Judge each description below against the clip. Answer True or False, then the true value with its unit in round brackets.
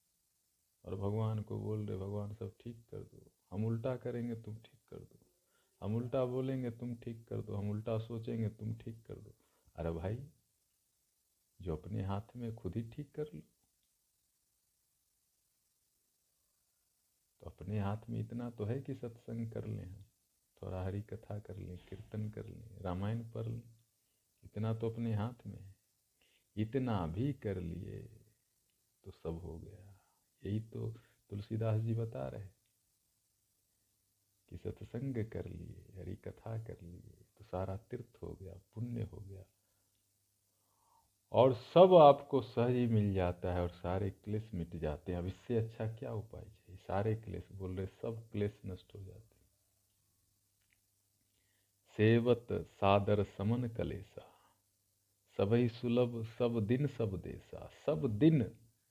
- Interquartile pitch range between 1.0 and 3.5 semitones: True (2.9 semitones)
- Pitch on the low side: True (105 Hz)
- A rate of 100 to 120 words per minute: False (145 wpm)